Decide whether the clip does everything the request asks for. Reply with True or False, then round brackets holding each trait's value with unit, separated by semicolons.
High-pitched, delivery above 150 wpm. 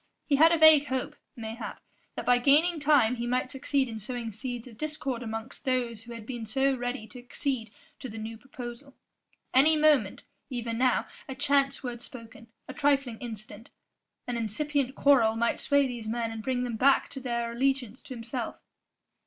True (250 Hz; 180 wpm)